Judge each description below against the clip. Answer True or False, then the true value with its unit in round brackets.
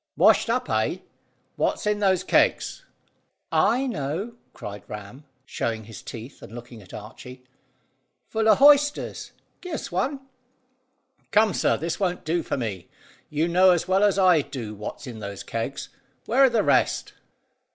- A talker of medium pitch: True (165 Hz)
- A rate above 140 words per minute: True (155 wpm)